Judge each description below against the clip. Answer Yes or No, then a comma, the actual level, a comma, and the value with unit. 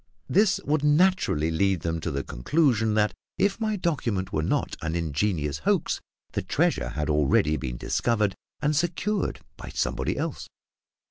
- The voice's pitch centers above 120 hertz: No, low, 100 Hz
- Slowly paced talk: No, average, 150 wpm